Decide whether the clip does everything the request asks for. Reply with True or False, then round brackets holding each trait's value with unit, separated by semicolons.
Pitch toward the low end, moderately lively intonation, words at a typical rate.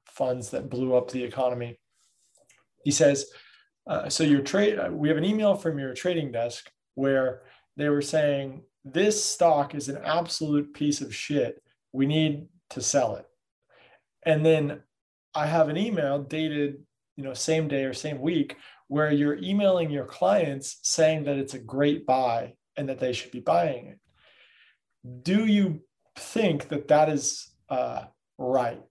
False (145 Hz; 3.1 semitones; 160 wpm)